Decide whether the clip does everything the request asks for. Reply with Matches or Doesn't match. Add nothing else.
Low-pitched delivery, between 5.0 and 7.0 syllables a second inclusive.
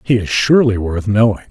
Matches